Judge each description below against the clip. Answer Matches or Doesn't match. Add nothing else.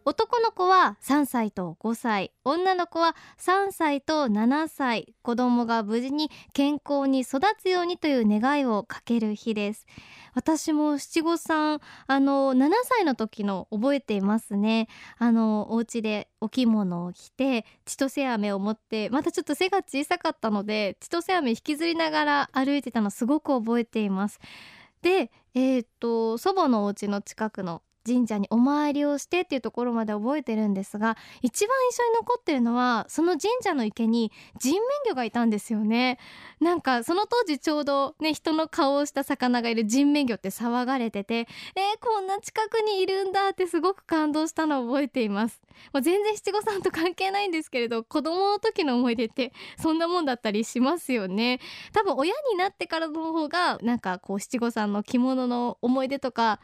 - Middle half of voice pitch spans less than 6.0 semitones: Doesn't match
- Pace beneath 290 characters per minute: Doesn't match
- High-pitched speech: Matches